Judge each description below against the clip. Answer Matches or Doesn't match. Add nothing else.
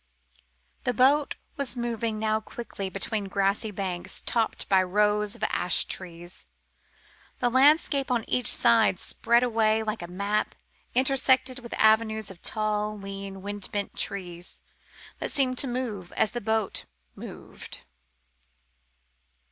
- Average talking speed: Doesn't match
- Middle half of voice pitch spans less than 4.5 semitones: Matches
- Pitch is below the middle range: Doesn't match